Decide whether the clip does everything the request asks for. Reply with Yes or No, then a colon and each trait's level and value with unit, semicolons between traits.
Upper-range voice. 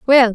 Yes: high, 240 Hz